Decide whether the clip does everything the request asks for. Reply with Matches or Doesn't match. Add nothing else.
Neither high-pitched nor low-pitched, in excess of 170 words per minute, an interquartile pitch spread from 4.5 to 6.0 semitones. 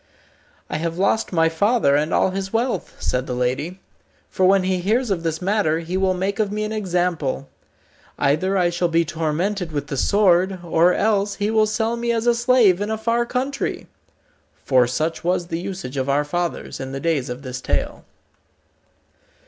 Matches